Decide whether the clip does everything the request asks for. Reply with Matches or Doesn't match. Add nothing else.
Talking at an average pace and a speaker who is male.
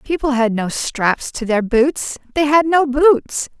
Doesn't match